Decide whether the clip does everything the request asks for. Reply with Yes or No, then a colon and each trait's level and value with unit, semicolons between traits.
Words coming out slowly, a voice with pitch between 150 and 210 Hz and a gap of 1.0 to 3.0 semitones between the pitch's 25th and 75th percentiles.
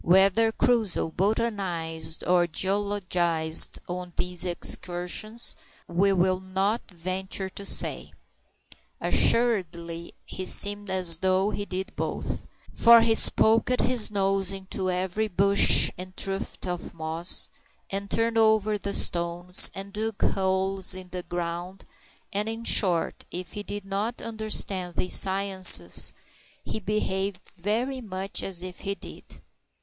Yes: slow, 125 wpm; high, 190 Hz; narrow, 2.5 semitones